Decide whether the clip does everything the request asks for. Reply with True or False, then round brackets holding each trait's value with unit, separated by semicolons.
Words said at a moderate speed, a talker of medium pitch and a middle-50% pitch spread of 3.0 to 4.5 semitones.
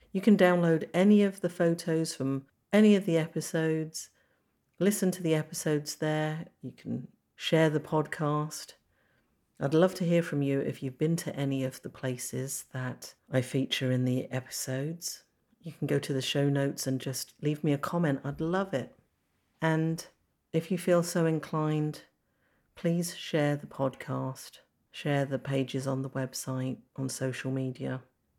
True (165 wpm; 150 Hz; 3.7 semitones)